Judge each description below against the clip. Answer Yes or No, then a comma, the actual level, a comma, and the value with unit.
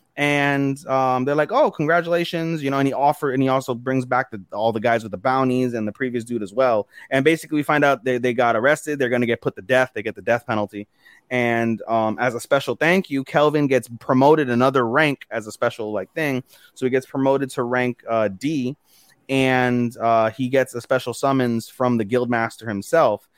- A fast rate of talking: Yes, fast, 220 wpm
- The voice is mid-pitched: No, low, 130 Hz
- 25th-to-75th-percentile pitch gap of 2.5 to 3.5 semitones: Yes, average, 2.8 semitones